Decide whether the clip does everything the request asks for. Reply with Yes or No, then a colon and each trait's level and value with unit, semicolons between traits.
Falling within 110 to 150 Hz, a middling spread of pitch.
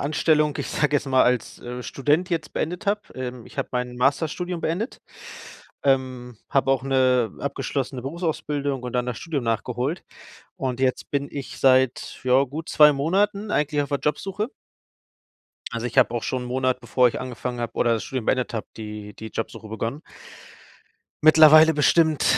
Yes: low, 135 Hz; average, 3.5 semitones